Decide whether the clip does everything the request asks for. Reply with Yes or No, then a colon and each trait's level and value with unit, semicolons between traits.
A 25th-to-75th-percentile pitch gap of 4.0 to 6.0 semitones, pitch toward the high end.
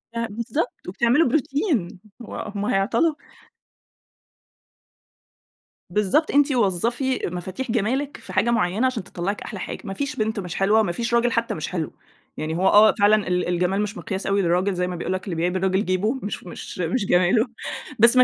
Yes: average, 4.5 semitones; high, 205 Hz